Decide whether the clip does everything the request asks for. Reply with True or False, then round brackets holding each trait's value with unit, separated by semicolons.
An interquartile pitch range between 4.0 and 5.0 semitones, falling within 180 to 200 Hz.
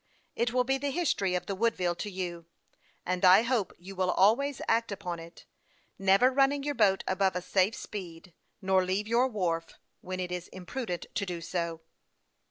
True (4.4 semitones; 190 Hz)